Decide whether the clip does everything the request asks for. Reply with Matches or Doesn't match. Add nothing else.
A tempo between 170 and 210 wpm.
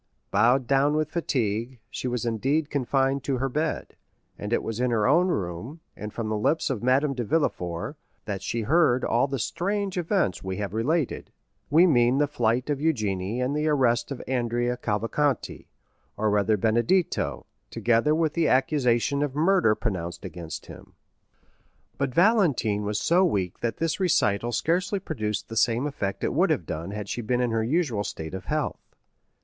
Matches